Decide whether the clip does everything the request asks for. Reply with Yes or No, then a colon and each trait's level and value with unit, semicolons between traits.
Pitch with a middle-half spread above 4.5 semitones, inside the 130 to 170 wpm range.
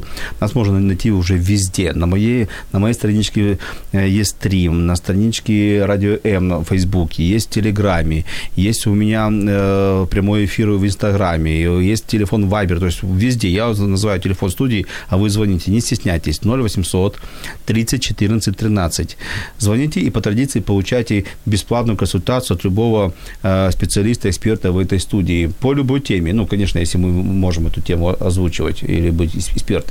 No: average, 3.0 semitones; average, 150 wpm